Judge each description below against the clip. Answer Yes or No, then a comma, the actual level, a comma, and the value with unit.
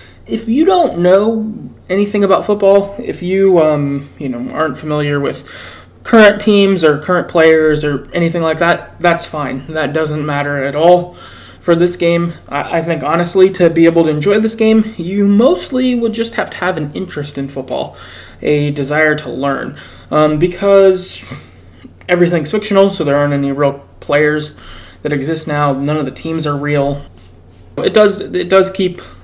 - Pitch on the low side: No, medium, 165 Hz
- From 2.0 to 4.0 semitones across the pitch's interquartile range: No, average, 4.7 semitones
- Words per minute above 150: Yes, average, 170 wpm